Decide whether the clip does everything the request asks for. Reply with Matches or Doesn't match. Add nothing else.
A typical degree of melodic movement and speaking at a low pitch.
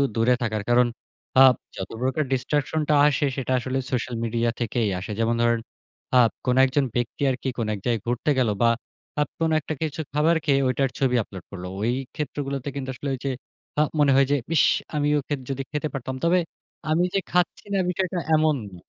Matches